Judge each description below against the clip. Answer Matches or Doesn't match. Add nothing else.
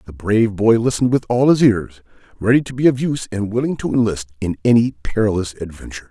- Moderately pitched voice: Doesn't match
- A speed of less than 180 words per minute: Doesn't match